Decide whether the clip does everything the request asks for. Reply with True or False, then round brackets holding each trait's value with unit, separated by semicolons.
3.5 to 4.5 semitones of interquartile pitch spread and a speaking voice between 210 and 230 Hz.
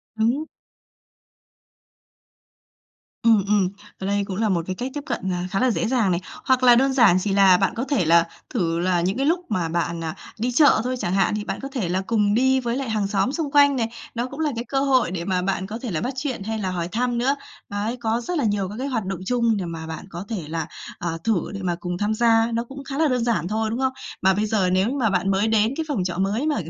False (5.1 semitones; 215 Hz)